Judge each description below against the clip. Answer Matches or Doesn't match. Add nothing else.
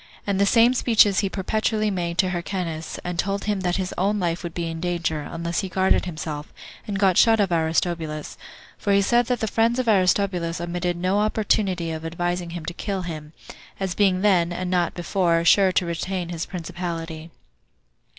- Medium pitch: Matches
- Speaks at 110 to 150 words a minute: Doesn't match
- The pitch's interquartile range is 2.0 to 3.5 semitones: Matches